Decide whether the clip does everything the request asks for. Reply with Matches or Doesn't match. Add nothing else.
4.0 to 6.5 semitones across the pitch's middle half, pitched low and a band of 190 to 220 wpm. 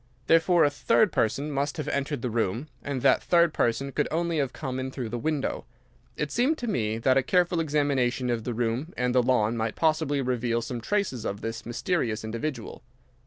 Matches